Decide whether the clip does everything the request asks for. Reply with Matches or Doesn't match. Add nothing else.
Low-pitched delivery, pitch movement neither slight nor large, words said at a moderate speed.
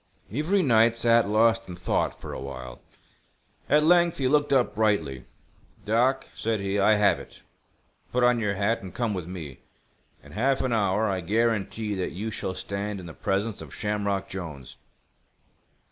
Matches